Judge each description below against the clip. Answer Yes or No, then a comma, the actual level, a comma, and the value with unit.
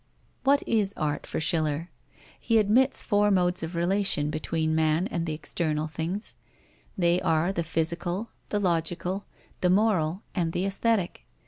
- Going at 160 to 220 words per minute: No, average, 140 wpm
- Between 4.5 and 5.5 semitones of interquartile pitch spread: No, average, 3.8 semitones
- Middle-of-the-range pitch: Yes, medium, 175 Hz